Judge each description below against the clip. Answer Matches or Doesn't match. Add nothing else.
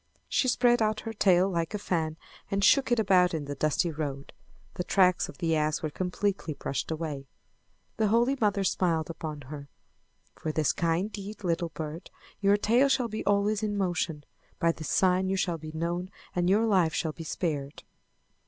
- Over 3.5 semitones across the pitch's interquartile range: Matches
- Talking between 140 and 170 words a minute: Doesn't match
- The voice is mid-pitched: Matches